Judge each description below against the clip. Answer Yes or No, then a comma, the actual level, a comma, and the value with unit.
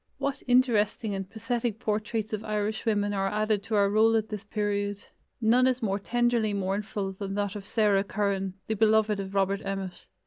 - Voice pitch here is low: No, high, 210 Hz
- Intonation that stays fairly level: Yes, narrow, 1.8 semitones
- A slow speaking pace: No, average, 175 wpm